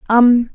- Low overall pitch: No, high, 235 Hz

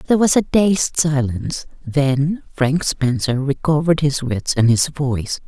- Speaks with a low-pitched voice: No, medium, 145 Hz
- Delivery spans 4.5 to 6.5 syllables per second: No, 4.3 syllables/s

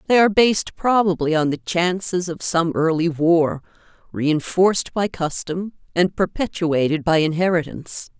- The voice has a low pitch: No, medium, 170 Hz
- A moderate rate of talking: No, slow, 130 wpm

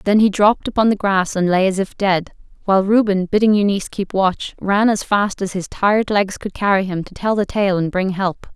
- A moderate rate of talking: No, fast, 240 wpm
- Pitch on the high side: Yes, high, 195 Hz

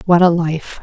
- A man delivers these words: No, female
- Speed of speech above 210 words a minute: Yes, fast, 220 wpm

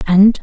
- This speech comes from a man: No, female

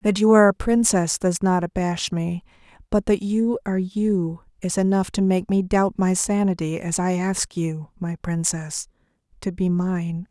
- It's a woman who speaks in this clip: Yes, female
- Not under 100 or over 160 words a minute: No, average, 180 wpm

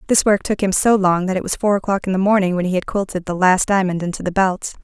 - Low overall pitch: No, high, 190 Hz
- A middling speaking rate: No, fast, 300 wpm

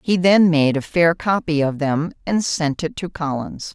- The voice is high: No, medium, 165 Hz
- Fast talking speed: Yes, fast, 210 wpm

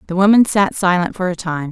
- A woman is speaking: Yes, female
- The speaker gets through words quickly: Yes, fast, 245 wpm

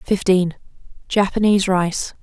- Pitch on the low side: No, high, 190 Hz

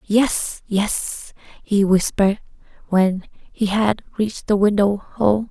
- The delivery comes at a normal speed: No, slow, 120 wpm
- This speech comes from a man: No, female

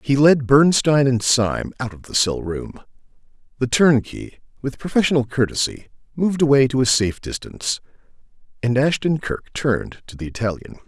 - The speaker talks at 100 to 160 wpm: Yes, average, 155 wpm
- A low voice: Yes, low, 130 Hz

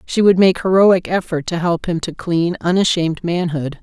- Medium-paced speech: Yes, average, 190 wpm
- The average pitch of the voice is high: No, medium, 175 Hz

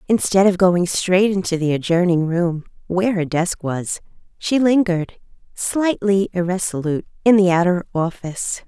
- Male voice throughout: No, female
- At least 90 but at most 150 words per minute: Yes, average, 140 wpm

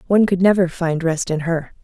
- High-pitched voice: No, medium, 175 Hz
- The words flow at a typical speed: No, fast, 230 wpm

